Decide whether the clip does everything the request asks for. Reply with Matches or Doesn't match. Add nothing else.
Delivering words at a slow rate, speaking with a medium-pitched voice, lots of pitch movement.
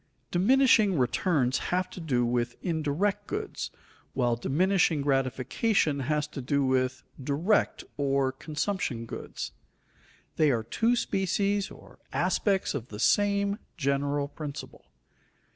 Matches